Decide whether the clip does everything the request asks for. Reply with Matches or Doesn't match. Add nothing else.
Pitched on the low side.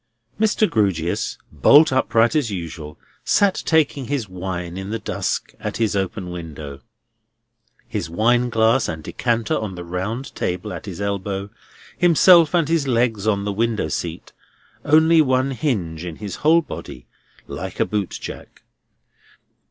Matches